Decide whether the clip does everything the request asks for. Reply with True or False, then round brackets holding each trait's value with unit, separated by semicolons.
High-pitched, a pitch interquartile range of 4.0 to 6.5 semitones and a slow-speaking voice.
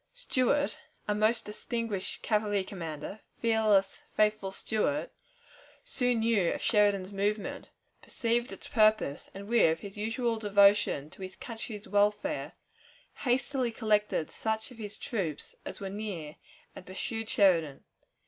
False (210 Hz; 2.7 semitones; 125 wpm)